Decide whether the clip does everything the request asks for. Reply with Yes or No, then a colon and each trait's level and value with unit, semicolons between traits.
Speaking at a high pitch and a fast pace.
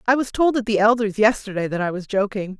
Yes: high, 215 Hz; fast, 255 wpm